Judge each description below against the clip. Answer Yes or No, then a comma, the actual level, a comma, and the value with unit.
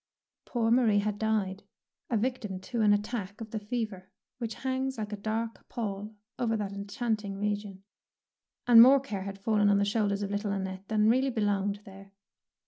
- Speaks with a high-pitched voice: Yes, high, 210 Hz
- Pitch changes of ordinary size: No, narrow, 2.3 semitones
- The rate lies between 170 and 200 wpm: Yes, average, 175 wpm